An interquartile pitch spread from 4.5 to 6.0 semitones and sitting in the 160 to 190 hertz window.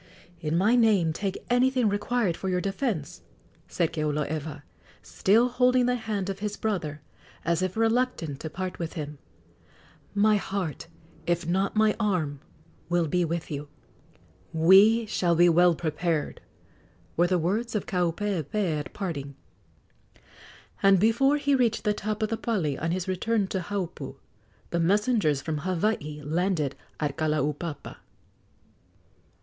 Yes: average, 5.0 semitones; medium, 185 Hz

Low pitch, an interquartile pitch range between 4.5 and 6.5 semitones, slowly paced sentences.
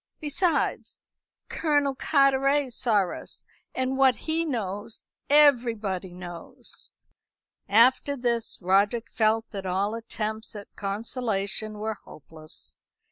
No: high, 225 Hz; average, 5.0 semitones; slow, 100 wpm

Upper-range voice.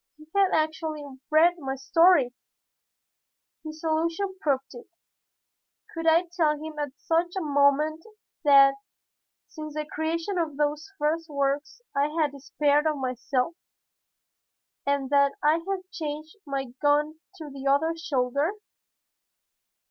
Yes: very high, 305 Hz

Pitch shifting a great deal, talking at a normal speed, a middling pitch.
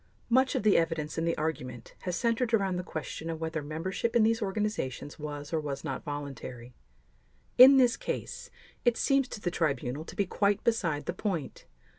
Yes: wide, 6.5 semitones; average, 185 wpm; medium, 165 Hz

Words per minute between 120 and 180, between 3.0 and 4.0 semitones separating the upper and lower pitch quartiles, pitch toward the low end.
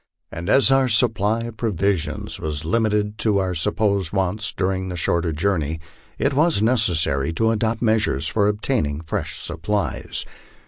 No: average, 150 wpm; average, 5.0 semitones; low, 100 Hz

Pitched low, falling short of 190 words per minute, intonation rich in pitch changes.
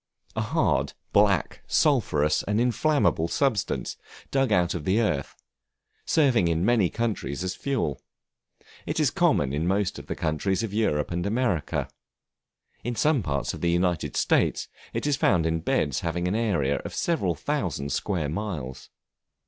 Yes: very low, 90 Hz; average, 155 wpm; wide, 6.1 semitones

